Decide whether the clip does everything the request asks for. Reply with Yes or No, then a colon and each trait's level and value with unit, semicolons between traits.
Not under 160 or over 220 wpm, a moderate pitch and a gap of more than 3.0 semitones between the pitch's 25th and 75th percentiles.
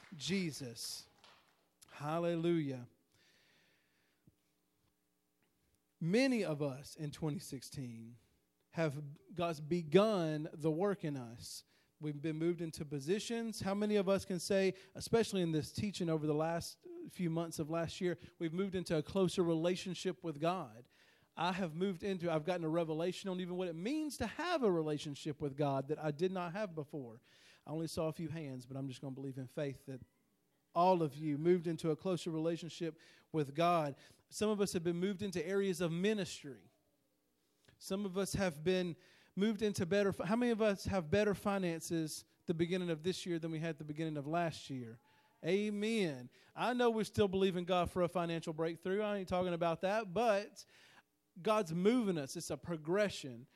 Yes: average, 175 wpm; medium, 170 Hz; average, 4.1 semitones